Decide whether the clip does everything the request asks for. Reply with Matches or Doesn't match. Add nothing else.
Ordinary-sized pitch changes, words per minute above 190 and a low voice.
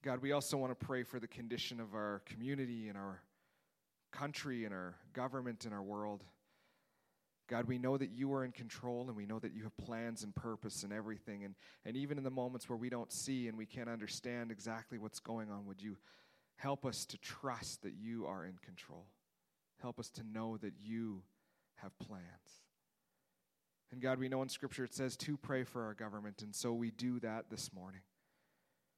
Matches